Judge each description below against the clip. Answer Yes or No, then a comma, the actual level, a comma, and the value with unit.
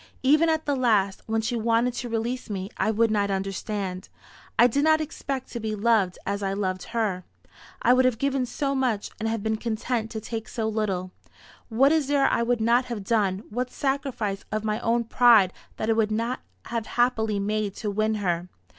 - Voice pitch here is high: Yes, high, 225 Hz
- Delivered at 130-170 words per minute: No, average, 200 wpm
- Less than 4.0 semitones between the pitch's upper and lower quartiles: Yes, average, 3.1 semitones